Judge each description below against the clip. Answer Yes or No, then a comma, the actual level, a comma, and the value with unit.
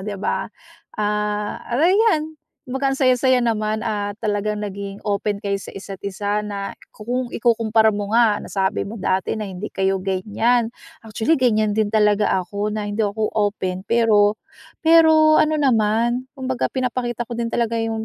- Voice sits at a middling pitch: No, high, 215 Hz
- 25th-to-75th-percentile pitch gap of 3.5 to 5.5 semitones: No, average, 2.8 semitones